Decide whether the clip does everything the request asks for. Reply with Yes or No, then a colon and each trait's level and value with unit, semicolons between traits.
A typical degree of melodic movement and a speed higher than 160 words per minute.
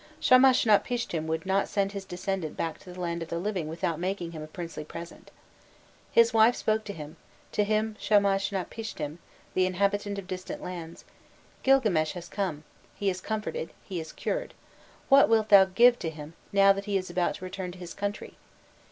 Yes: average, 3.6 semitones; average, 180 wpm